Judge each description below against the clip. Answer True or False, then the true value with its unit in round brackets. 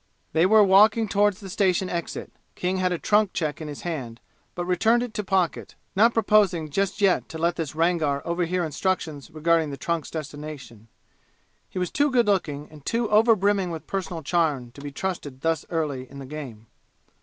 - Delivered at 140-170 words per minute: False (190 wpm)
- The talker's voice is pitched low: False (170 Hz)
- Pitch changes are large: False (4.5 semitones)